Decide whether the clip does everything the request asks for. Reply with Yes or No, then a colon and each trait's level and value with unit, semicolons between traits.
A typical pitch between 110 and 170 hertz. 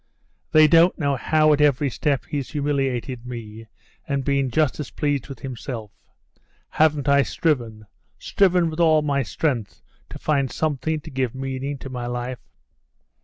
Yes: medium, 140 Hz